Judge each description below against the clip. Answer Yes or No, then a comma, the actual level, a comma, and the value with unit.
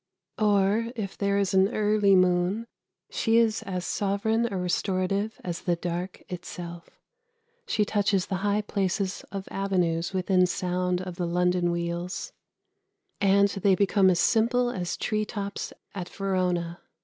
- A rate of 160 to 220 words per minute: No, average, 140 wpm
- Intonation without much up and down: Yes, narrow, 2.3 semitones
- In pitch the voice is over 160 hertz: Yes, high, 190 Hz